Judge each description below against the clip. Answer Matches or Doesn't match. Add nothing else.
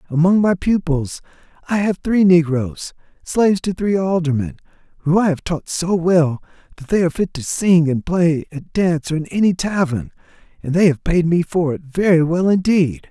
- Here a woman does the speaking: Doesn't match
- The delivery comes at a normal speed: Matches